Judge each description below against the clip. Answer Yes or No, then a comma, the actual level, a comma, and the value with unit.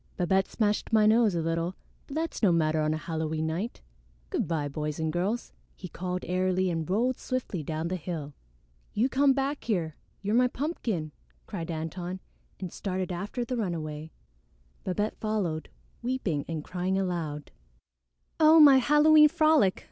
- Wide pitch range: Yes, wide, 6.4 semitones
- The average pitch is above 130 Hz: Yes, medium, 185 Hz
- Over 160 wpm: No, average, 155 wpm